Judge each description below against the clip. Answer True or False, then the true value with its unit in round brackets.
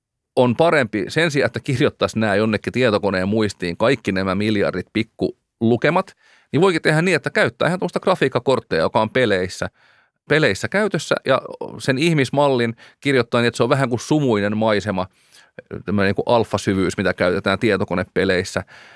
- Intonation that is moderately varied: True (4.1 semitones)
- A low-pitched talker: True (115 Hz)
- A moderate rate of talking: True (140 wpm)